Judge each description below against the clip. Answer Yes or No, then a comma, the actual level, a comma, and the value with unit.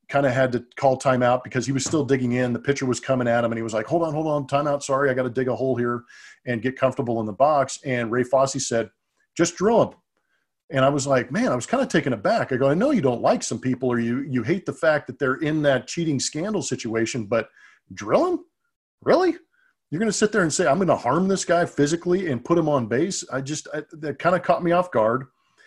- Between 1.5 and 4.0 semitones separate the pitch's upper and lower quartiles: No, average, 5.1 semitones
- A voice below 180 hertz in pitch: Yes, medium, 140 Hz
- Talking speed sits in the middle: No, fast, 270 wpm